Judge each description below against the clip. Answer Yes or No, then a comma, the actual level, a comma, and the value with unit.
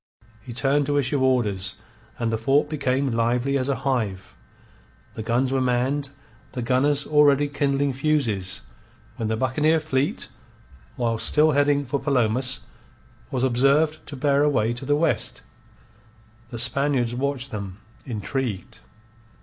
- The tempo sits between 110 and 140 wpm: Yes, slow, 135 wpm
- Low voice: Yes, low, 130 Hz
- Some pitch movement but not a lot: Yes, average, 3.1 semitones